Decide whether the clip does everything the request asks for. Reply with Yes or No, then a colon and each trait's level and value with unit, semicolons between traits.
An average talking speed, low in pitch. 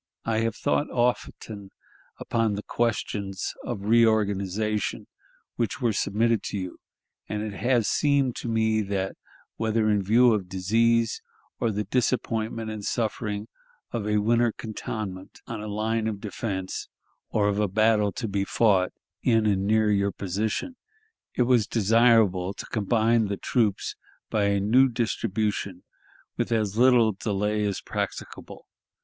Yes: average, 145 wpm; low, 110 Hz